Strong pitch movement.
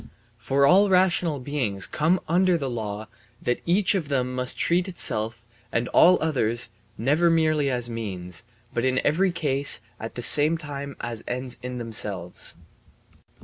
Yes: wide, 5.8 semitones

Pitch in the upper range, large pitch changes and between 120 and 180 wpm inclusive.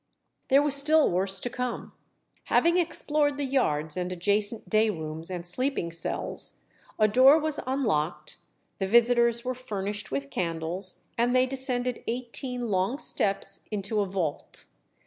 Yes: high, 220 Hz; wide, 5.9 semitones; average, 145 wpm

